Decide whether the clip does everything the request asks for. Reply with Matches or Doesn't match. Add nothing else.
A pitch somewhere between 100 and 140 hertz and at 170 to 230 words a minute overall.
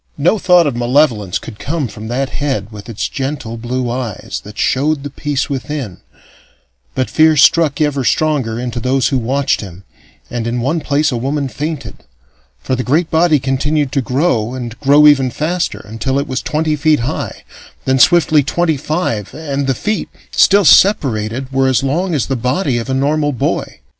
Matches